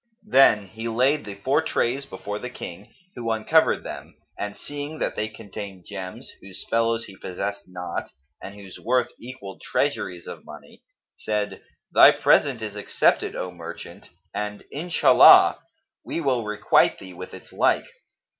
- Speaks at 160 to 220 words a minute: No, average, 150 wpm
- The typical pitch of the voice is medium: No, low, 105 Hz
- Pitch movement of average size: Yes, average, 4.2 semitones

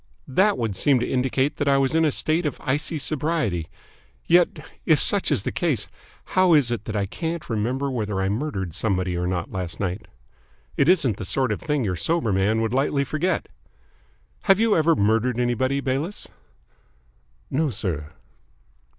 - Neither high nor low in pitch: No, low, 130 Hz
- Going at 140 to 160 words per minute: No, average, 175 wpm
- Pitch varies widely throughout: Yes, wide, 6.7 semitones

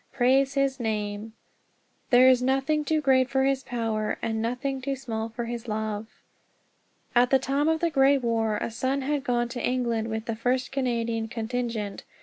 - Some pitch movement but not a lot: Yes, average, 3.0 semitones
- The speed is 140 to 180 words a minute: Yes, average, 175 wpm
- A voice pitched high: Yes, high, 245 Hz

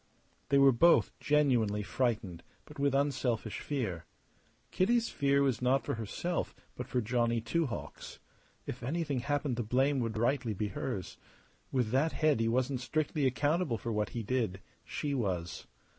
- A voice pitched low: Yes, low, 125 Hz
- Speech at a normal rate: Yes, average, 160 wpm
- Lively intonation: No, average, 4.0 semitones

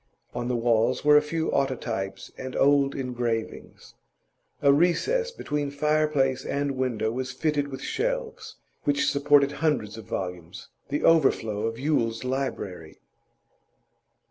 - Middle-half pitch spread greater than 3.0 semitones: Yes, average, 4.3 semitones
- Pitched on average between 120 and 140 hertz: Yes, low, 135 Hz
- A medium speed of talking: No, slow, 125 wpm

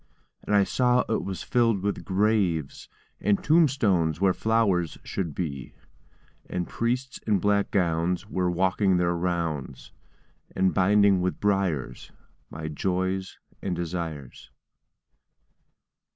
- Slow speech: Yes, slow, 115 wpm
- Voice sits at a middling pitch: No, very low, 95 Hz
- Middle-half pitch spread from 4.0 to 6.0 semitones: No, average, 3.2 semitones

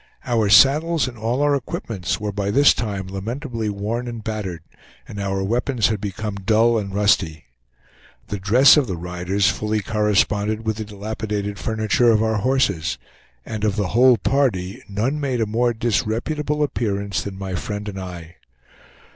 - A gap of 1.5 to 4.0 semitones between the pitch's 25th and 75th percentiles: Yes, average, 3.1 semitones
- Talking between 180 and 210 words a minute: No, average, 165 wpm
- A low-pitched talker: Yes, low, 105 Hz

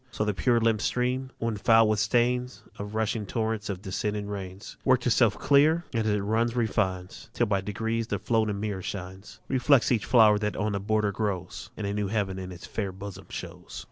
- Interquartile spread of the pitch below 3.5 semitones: Yes, narrow, 2.6 semitones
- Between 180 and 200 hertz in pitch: No, low, 105 Hz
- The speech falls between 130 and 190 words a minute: No, fast, 205 wpm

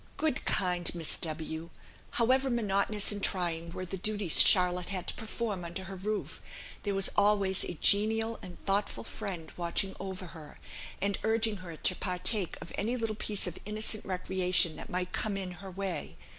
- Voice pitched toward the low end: No, high, 190 Hz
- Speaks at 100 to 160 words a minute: No, average, 170 wpm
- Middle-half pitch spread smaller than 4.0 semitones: Yes, average, 2.9 semitones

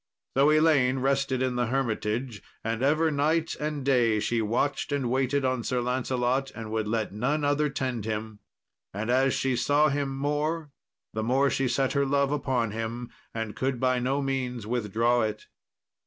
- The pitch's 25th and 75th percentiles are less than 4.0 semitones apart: Yes, average, 3.3 semitones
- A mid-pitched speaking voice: No, low, 130 Hz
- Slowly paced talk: No, average, 170 wpm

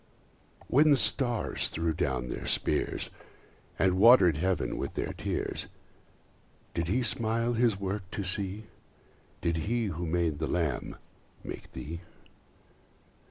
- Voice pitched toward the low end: Yes, very low, 95 Hz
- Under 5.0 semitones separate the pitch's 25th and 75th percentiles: No, wide, 5.5 semitones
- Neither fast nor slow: No, slow, 125 wpm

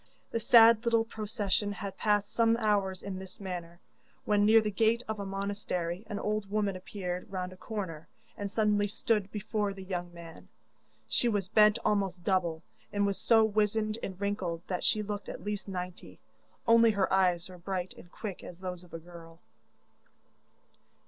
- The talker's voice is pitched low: No, high, 200 Hz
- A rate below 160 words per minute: No, average, 175 wpm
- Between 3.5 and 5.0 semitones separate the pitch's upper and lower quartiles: No, average, 2.7 semitones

